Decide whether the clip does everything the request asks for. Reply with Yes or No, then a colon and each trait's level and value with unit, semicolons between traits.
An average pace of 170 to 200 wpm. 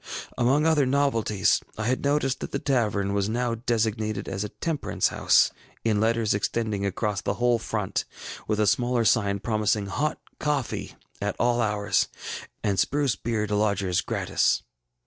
No: average, 155 wpm